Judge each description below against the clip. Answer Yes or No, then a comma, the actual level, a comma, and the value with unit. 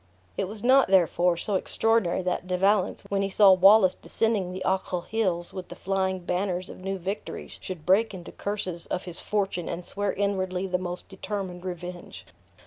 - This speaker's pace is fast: No, average, 180 wpm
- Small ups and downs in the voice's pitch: Yes, narrow, 1.9 semitones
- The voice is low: No, high, 190 Hz